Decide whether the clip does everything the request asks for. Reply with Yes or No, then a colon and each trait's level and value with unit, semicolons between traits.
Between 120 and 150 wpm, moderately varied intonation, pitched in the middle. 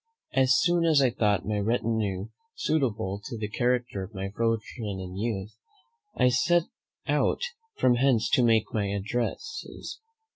No: average, 145 wpm; average, 3.7 semitones; low, 115 Hz